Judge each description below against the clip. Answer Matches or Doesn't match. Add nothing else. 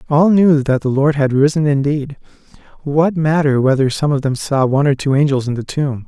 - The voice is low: Doesn't match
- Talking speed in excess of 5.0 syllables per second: Matches